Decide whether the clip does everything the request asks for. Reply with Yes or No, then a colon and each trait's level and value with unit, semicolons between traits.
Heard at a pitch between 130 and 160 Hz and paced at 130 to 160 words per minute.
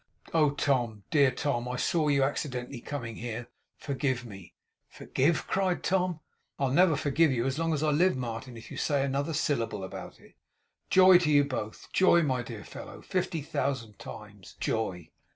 No: medium, 140 Hz; average, 170 wpm